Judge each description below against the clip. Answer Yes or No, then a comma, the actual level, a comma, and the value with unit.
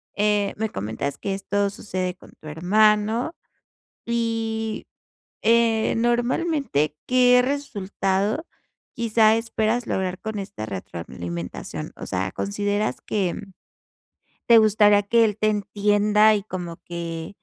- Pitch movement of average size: Yes, average, 3.2 semitones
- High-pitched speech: Yes, high, 210 Hz